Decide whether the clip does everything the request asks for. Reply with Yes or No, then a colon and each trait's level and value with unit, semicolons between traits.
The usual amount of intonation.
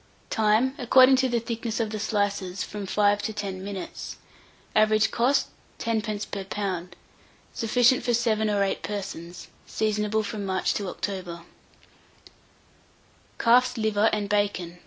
No: narrow, 2.3 semitones